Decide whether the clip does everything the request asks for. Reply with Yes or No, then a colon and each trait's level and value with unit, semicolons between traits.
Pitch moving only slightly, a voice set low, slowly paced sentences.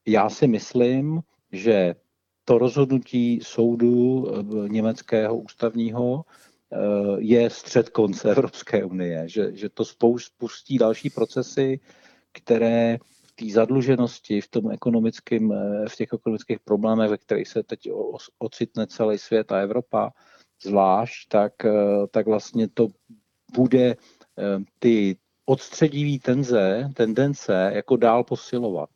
No: average, 3.0 semitones; low, 115 Hz; slow, 110 wpm